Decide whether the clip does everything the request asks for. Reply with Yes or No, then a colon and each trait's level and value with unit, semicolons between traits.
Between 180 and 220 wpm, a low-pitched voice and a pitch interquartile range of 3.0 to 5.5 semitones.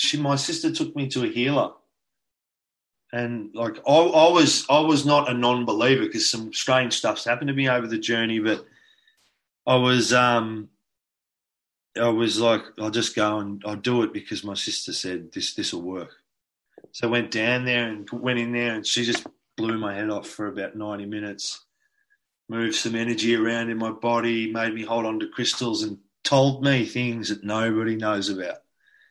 No: average, 185 wpm; low, 115 Hz; narrow, 2.6 semitones